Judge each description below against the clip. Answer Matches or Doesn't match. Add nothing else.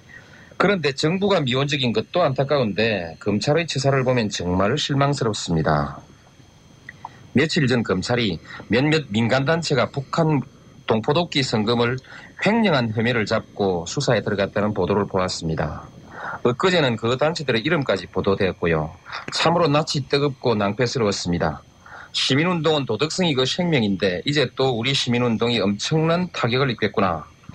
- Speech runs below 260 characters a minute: Doesn't match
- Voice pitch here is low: Matches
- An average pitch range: Doesn't match